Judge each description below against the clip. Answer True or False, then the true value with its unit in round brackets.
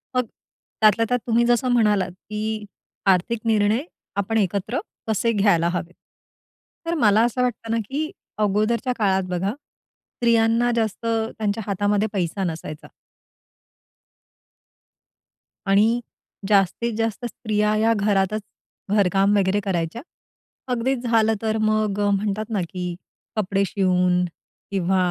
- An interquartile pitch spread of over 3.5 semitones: False (2.7 semitones)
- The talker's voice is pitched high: True (210 Hz)